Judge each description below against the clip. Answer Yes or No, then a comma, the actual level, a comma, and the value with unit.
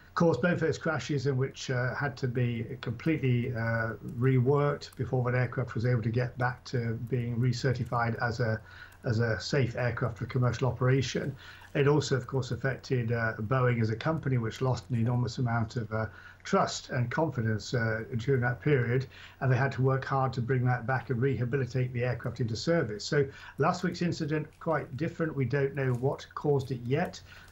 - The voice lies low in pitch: Yes, low, 130 Hz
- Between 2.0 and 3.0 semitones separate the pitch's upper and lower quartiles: Yes, narrow, 2.4 semitones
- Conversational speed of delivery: Yes, average, 190 wpm